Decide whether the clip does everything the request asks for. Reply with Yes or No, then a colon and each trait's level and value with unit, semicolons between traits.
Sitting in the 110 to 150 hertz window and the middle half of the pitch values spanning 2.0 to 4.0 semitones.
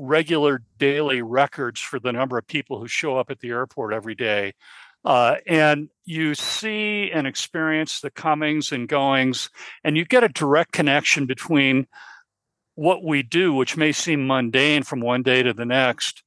Yes: medium, 140 Hz; average, 3.3 semitones